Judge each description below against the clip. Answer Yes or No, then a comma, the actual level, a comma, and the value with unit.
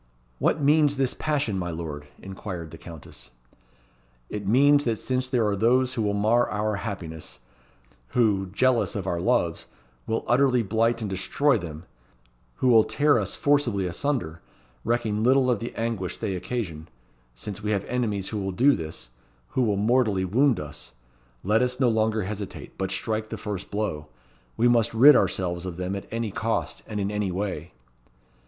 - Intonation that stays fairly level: No, average, 4.4 semitones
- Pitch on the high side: No, low, 105 Hz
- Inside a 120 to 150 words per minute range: No, average, 170 wpm